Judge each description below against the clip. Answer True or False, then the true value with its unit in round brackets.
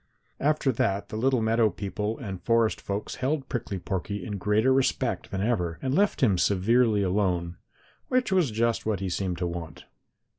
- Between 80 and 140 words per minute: False (175 wpm)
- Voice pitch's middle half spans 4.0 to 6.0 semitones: True (4.4 semitones)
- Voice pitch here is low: True (105 Hz)